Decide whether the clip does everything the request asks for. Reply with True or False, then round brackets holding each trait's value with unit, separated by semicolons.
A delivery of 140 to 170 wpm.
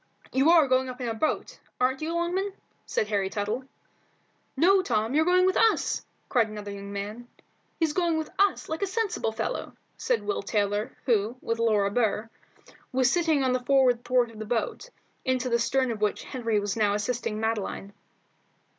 False (180 wpm)